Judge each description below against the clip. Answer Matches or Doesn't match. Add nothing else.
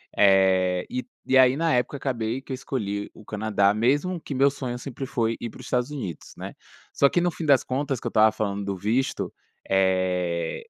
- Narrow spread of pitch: Doesn't match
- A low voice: Matches